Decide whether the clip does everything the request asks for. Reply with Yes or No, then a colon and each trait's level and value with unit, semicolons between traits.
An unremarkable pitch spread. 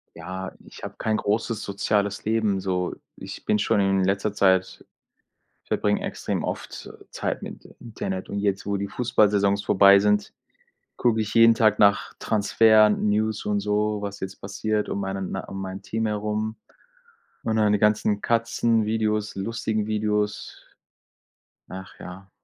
No: narrow, 1.6 semitones